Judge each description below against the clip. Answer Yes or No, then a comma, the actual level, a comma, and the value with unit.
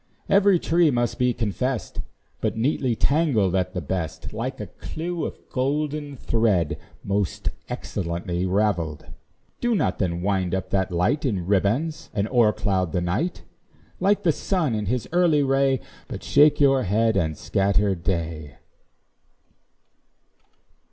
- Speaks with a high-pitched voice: No, low, 110 Hz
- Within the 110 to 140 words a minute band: Yes, slow, 135 wpm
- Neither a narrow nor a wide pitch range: No, wide, 7.6 semitones